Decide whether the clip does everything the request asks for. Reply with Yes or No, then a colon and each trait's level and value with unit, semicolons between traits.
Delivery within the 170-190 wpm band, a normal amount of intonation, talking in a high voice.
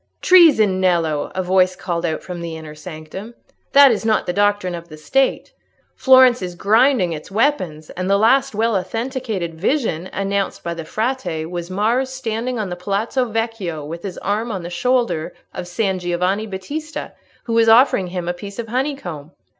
Yes: average, 180 wpm; average, 5.0 semitones; high, 195 Hz